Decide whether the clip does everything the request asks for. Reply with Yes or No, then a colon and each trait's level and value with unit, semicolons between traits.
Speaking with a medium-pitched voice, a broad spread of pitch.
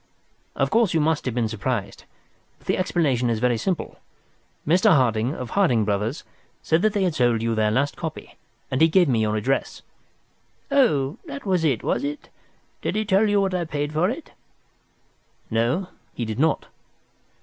Yes: medium, 150 Hz; wide, 7.9 semitones